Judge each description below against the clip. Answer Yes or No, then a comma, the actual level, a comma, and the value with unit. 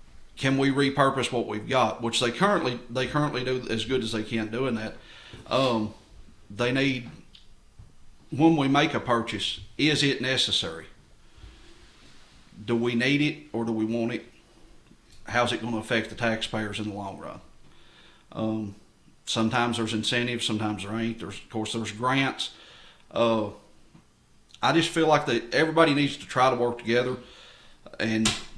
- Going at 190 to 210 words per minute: No, average, 160 wpm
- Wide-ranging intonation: No, average, 3.0 semitones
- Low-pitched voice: Yes, low, 120 Hz